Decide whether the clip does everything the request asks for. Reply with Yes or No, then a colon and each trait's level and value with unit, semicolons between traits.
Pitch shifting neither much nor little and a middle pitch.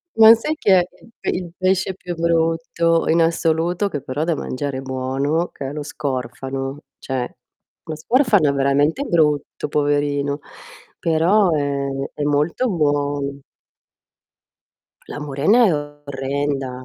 Yes: average, 3.2 semitones; medium, 150 Hz